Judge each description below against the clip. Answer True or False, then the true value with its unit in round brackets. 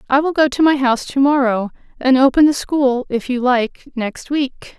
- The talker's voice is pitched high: True (265 Hz)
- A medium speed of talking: False (215 wpm)